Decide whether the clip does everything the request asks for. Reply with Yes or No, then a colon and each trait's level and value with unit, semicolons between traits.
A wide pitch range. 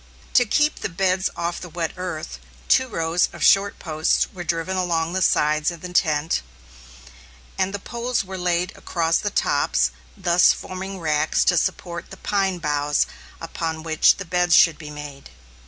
No: average, 2.8 semitones